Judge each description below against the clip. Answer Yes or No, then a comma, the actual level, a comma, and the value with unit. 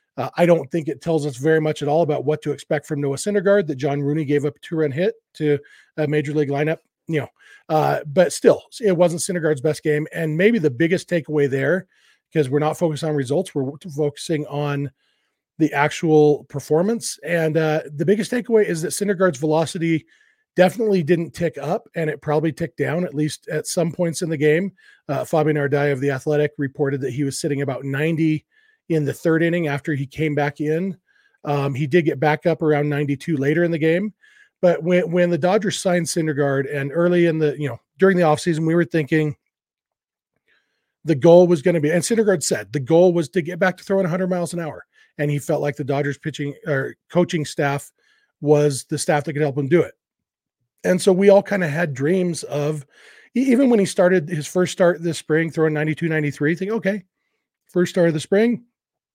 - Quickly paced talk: Yes, fast, 210 wpm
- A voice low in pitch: No, medium, 160 Hz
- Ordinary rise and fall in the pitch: Yes, average, 3.3 semitones